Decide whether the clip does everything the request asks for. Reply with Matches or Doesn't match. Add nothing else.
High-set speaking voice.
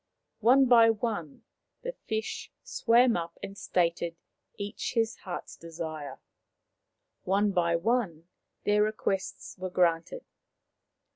Matches